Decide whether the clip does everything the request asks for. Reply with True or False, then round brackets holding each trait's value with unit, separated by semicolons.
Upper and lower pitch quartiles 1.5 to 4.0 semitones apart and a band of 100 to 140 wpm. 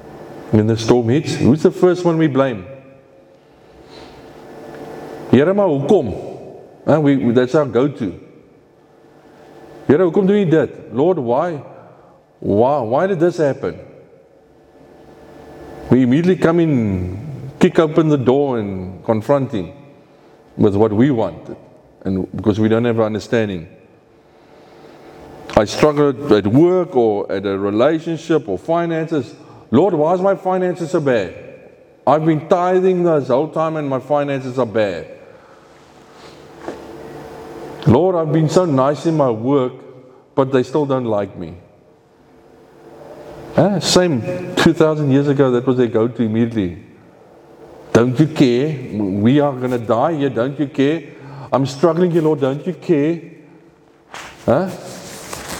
False (5.2 semitones; 135 wpm)